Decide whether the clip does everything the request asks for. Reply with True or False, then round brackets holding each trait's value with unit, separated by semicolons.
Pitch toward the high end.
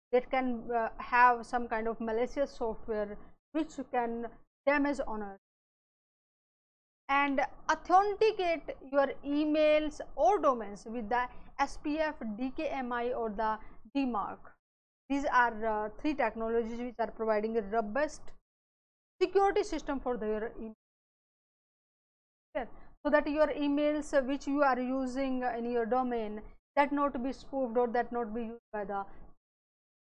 True (250 Hz)